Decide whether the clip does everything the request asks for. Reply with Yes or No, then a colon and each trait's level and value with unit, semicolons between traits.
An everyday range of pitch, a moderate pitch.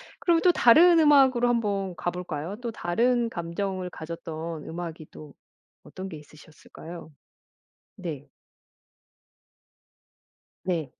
No: wide, 6.4 semitones; medium, 180 Hz